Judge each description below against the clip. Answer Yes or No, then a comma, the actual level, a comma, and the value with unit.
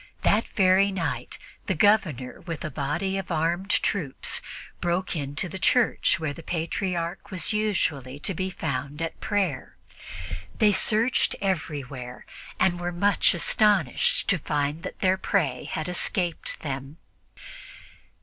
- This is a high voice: No, medium, 175 Hz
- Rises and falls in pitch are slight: No, average, 4.7 semitones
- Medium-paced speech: No, slow, 130 wpm